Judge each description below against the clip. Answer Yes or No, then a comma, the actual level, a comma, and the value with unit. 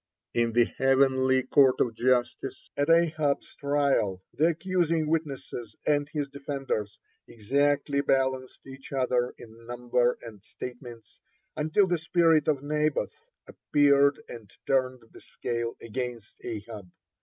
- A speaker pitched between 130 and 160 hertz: Yes, low, 135 Hz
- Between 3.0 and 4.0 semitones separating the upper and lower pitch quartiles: Yes, average, 3.3 semitones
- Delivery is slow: Yes, slow, 130 wpm